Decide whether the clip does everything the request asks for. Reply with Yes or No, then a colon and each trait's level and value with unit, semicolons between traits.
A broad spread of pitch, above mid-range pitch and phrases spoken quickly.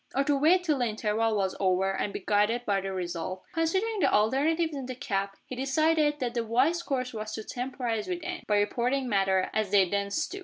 Yes: wide, 6.3 semitones; high, 240 Hz; fast, 220 wpm